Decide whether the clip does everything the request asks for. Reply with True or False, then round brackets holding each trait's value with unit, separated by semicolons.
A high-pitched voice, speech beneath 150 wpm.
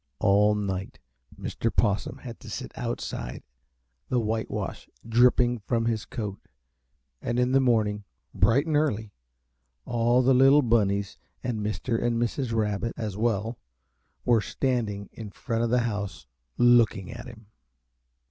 False (115 Hz; 140 wpm)